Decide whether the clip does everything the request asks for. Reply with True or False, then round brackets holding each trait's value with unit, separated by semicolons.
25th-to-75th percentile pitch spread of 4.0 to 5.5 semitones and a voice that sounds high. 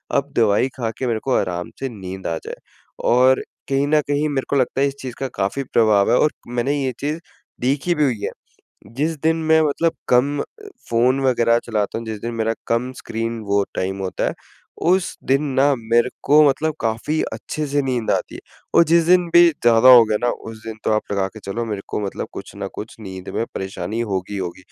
False (4.4 semitones; 120 Hz)